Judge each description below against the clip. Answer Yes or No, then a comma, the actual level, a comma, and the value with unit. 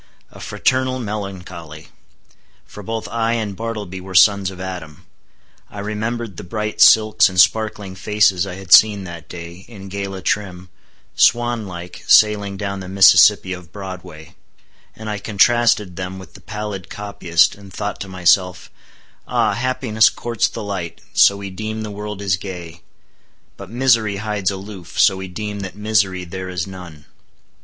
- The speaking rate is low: No, average, 155 wpm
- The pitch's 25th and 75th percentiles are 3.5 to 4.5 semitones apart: No, narrow, 2.6 semitones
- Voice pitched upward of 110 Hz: No, low, 100 Hz